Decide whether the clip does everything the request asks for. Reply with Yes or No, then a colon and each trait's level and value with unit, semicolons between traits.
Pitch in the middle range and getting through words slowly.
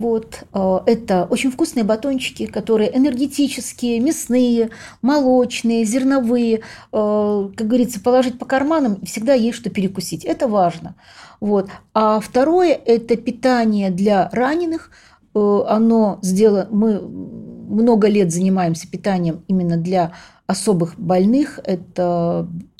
No: high, 220 Hz; slow, 105 wpm